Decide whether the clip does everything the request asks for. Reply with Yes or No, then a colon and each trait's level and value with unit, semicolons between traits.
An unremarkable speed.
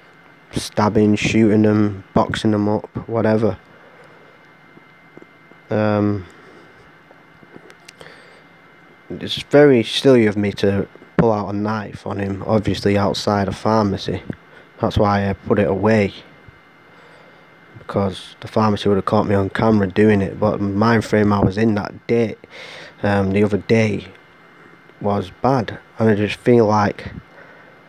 No: slow, 130 wpm